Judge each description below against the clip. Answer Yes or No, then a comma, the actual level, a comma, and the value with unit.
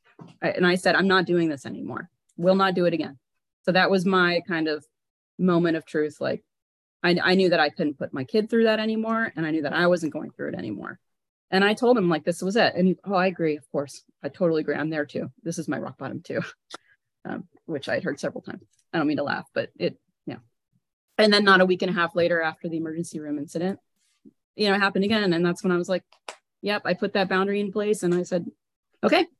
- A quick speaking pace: Yes, fast, 250 wpm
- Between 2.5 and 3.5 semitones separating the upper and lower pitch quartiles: Yes, average, 2.9 semitones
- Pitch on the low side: No, medium, 180 Hz